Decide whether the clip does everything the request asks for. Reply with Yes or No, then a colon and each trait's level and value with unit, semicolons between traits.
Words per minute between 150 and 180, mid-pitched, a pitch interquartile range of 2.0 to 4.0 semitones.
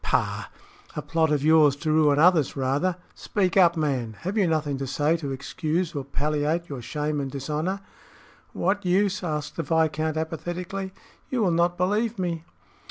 Yes: average, 165 wpm; medium, 160 Hz; average, 3.5 semitones